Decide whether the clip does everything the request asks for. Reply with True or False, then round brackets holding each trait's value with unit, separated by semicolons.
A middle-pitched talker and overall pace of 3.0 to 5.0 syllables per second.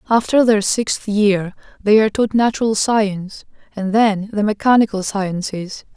False (210 Hz; 4.5 syllables/s)